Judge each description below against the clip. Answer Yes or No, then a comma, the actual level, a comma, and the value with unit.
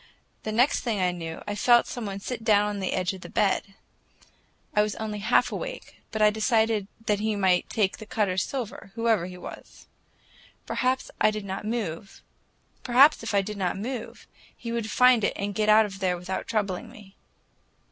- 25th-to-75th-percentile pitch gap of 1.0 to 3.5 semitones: Yes, narrow, 2.6 semitones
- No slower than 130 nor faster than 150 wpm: No, average, 170 wpm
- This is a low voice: No, high, 210 Hz